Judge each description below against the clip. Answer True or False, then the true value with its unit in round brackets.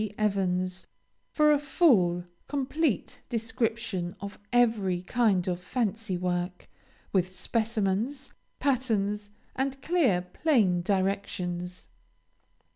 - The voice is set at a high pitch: True (205 Hz)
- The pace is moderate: False (90 wpm)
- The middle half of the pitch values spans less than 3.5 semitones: False (5.1 semitones)